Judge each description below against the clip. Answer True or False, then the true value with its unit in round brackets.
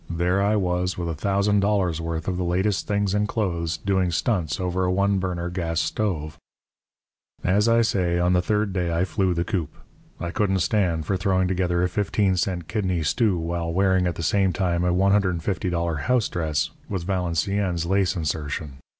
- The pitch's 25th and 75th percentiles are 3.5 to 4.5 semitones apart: False (2.6 semitones)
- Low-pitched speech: True (90 Hz)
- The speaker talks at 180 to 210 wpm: True (185 wpm)